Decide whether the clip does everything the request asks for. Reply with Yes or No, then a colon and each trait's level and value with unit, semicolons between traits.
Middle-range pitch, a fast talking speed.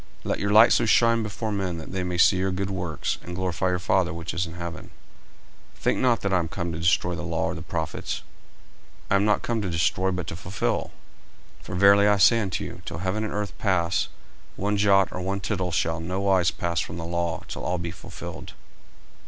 No: very low, 95 Hz; fast, 235 wpm